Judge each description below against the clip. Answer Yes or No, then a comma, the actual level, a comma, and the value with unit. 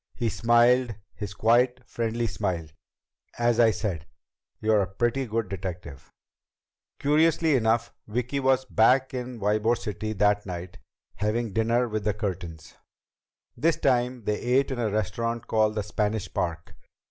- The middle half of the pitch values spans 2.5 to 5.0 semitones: Yes, average, 2.9 semitones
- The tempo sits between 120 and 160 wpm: Yes, average, 140 wpm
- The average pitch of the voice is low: Yes, low, 110 Hz